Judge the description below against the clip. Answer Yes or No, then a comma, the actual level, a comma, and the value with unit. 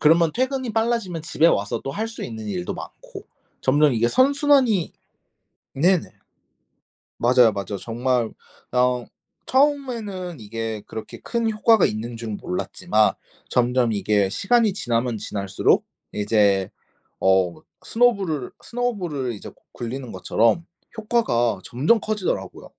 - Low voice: Yes, low, 130 Hz